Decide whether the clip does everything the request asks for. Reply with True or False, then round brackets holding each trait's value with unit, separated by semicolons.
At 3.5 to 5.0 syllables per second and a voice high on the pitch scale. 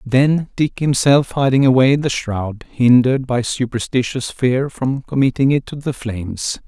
False (4.4 syllables/s; 130 Hz)